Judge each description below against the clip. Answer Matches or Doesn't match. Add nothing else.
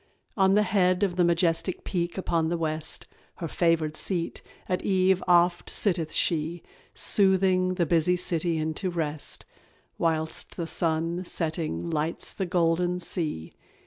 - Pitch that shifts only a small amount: Matches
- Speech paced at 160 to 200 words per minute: Doesn't match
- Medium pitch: Matches